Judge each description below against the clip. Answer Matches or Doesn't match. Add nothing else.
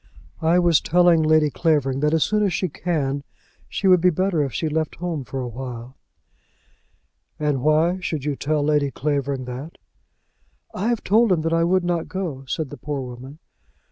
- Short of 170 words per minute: Doesn't match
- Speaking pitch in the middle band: Matches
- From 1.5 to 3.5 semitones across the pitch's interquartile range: Doesn't match